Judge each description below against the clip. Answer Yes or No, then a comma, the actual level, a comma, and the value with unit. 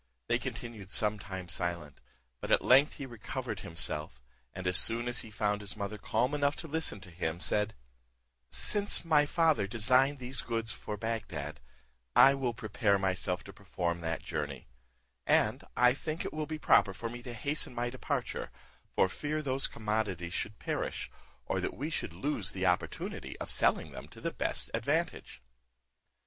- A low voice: Yes, low, 110 Hz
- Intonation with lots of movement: Yes, wide, 5.9 semitones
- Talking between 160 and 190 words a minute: Yes, average, 170 wpm